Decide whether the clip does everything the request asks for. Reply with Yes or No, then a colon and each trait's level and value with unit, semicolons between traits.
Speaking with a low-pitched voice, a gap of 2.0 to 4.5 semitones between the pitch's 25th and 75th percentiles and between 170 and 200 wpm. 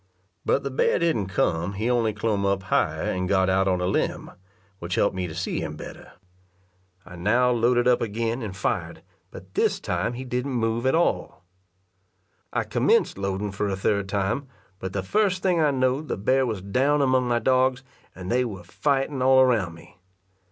No: low, 115 Hz; average, 5.1 semitones; average, 190 wpm